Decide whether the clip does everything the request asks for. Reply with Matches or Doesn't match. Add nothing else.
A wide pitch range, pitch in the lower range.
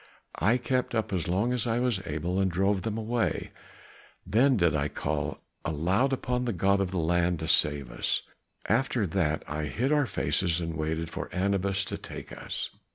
Matches